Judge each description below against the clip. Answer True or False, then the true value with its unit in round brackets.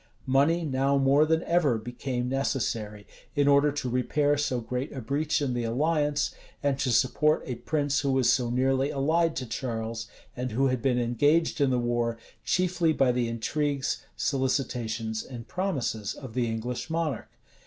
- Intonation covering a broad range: False (3.3 semitones)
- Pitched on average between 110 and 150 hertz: True (135 Hz)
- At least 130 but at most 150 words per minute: False (165 wpm)